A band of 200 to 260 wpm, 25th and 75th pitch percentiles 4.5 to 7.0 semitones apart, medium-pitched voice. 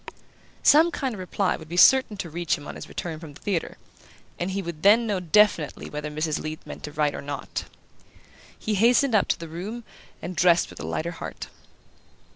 Yes: fast, 205 wpm; average, 5.1 semitones; medium, 175 Hz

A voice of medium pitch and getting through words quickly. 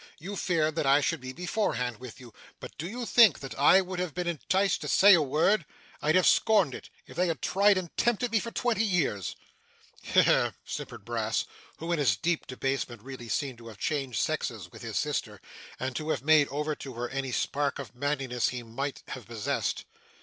Yes: medium, 150 Hz; fast, 210 wpm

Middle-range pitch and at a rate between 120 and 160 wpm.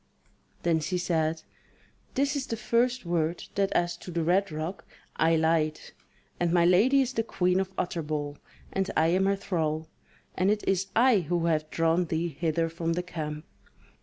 No: medium, 170 Hz; average, 175 wpm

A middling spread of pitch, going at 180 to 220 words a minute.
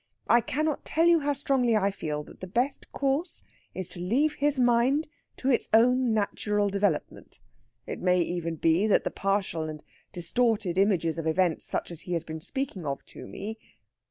No: wide, 6.7 semitones; average, 185 wpm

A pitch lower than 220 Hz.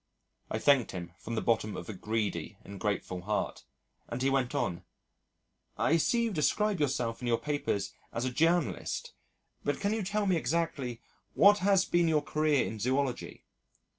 Yes: low, 135 Hz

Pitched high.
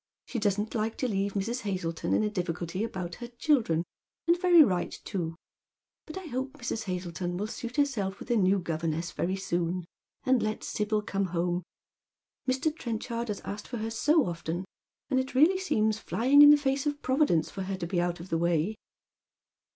Yes: high, 210 Hz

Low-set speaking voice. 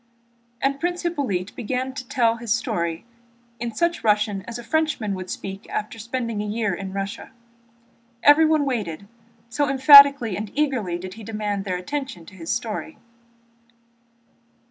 No: high, 230 Hz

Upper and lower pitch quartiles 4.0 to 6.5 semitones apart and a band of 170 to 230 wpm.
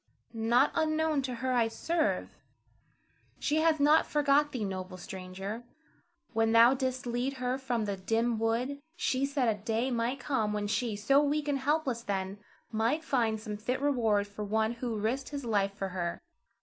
Yes: average, 4.4 semitones; average, 175 wpm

